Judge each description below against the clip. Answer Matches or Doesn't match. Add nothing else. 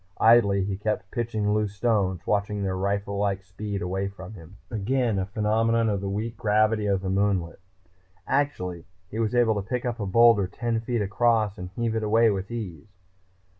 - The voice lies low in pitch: Matches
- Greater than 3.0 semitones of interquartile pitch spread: Doesn't match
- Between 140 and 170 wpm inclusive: Doesn't match